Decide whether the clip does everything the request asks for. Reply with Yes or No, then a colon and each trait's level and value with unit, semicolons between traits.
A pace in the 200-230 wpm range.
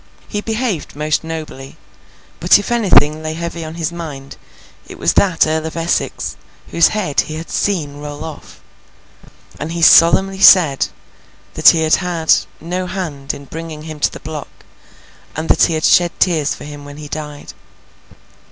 No: average, 170 wpm